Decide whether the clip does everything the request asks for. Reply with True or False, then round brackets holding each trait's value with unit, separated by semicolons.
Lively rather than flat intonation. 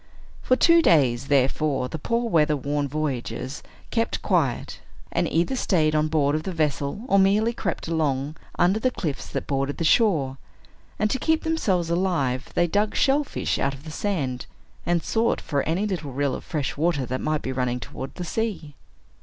True (6.1 semitones)